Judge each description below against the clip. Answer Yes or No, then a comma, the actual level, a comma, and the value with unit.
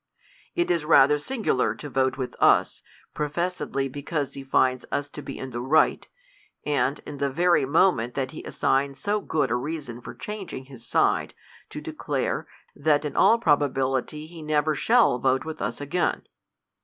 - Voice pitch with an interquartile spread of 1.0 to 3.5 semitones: Yes, average, 3.1 semitones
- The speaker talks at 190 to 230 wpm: No, average, 170 wpm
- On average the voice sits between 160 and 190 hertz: No, medium, 145 Hz